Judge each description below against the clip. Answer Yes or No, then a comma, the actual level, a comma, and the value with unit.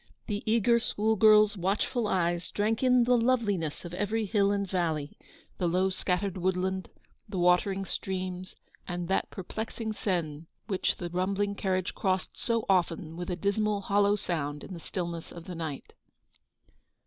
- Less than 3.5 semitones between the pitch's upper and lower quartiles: Yes, average, 2.9 semitones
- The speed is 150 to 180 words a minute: Yes, average, 155 wpm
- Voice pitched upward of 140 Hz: Yes, high, 190 Hz